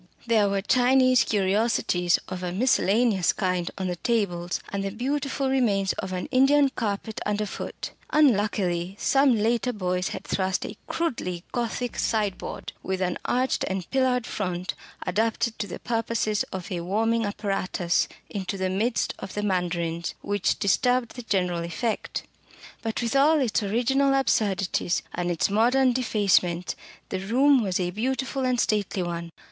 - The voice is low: No, high, 205 Hz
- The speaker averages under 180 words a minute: Yes, average, 150 wpm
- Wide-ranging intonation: No, average, 4.9 semitones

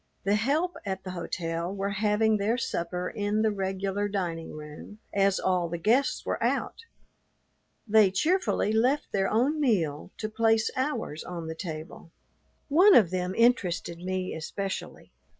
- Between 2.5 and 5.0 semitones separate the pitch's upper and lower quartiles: Yes, average, 3.7 semitones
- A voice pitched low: No, high, 200 Hz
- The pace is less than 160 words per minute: Yes, average, 150 wpm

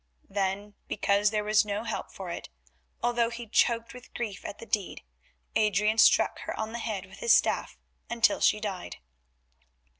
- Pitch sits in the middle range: No, high, 215 Hz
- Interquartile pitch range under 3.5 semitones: Yes, narrow, 2.4 semitones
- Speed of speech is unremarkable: Yes, average, 170 wpm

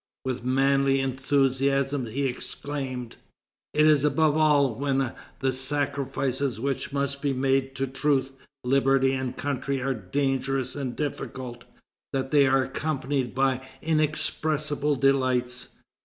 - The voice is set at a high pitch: No, low, 135 Hz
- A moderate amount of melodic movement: No, narrow, 1.4 semitones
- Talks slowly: Yes, slow, 120 wpm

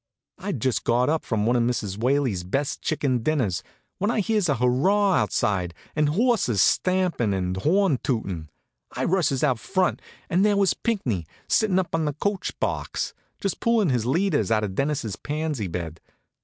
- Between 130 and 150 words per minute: No, average, 175 wpm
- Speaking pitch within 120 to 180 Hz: Yes, medium, 140 Hz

